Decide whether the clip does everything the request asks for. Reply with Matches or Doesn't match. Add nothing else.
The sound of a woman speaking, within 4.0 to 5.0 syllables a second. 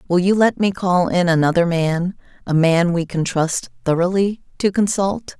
Matches